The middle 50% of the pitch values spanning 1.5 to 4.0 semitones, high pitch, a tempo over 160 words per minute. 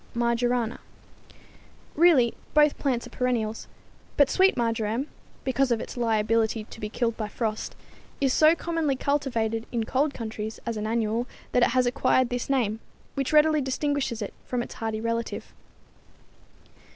No: average, 3.4 semitones; high, 240 Hz; average, 150 wpm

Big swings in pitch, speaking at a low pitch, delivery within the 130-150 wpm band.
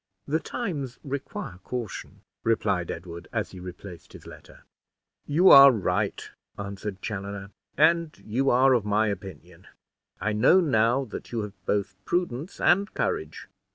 Yes: wide, 6.1 semitones; low, 110 Hz; average, 140 wpm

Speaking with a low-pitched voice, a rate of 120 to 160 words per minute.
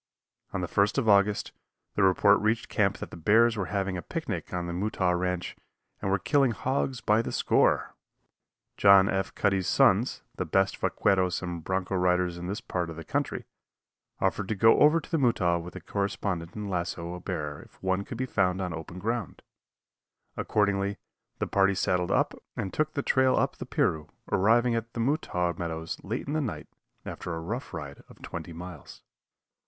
No: very low, 95 Hz; average, 190 wpm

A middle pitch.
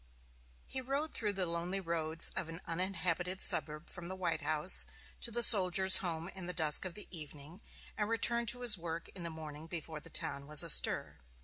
Yes: medium, 175 Hz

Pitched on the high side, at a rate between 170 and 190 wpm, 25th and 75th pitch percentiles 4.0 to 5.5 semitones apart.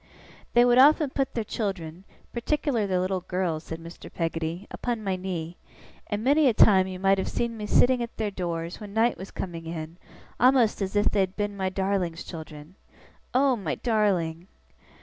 Yes: high, 195 Hz; average, 180 wpm; average, 4.8 semitones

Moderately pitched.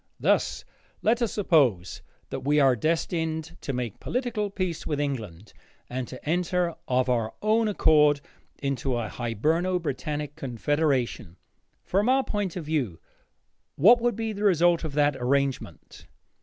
Yes: medium, 150 Hz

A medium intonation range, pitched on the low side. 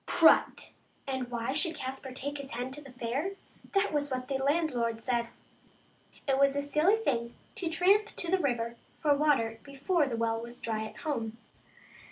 No: average, 4.3 semitones; very high, 270 Hz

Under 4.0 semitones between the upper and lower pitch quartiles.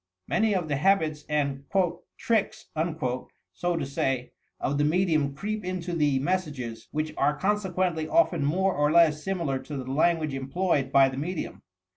No: average, 4.7 semitones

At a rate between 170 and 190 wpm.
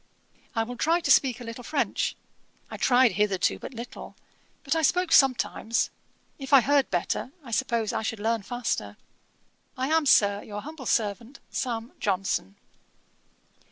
No: average, 155 wpm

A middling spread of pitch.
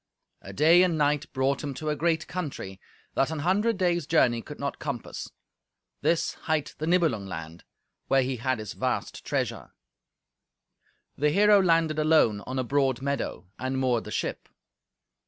Yes: average, 4.2 semitones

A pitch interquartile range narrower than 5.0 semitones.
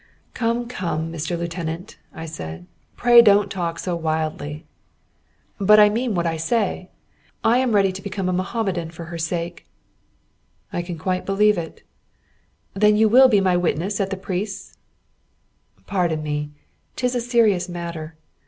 Yes: average, 4.0 semitones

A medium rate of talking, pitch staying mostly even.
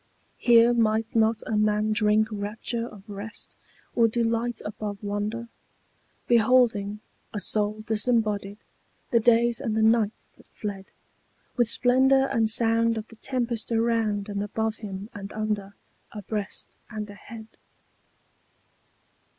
No: slow, 125 wpm; narrow, 1.8 semitones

